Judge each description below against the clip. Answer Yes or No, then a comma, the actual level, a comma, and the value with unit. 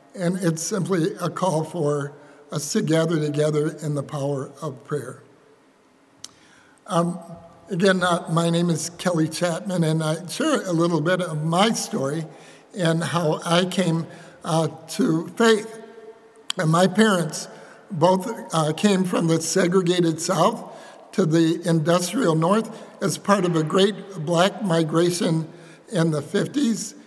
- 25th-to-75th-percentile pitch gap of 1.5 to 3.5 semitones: Yes, average, 3.0 semitones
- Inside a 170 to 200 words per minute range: No, average, 140 wpm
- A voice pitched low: No, medium, 170 Hz